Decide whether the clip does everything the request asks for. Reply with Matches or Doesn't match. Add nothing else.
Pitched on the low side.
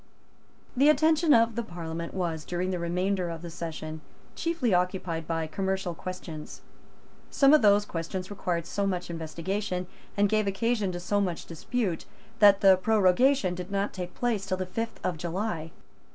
Doesn't match